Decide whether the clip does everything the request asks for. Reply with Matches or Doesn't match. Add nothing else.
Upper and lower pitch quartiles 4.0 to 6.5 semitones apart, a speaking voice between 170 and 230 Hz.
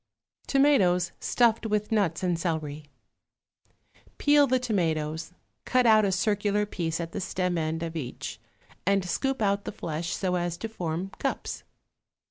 Matches